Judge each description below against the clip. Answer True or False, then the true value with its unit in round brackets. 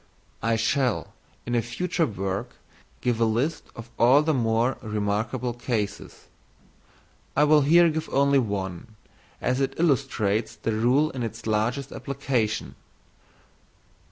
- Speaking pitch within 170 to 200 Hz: False (120 Hz)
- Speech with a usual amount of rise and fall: True (4.1 semitones)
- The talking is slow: True (130 wpm)